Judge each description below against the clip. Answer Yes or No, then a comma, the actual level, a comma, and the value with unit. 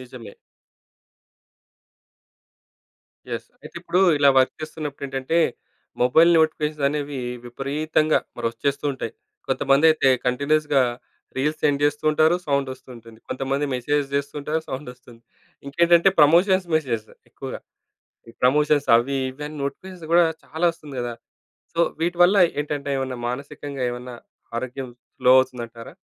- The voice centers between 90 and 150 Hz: Yes, medium, 140 Hz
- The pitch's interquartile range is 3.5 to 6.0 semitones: No, average, 3.1 semitones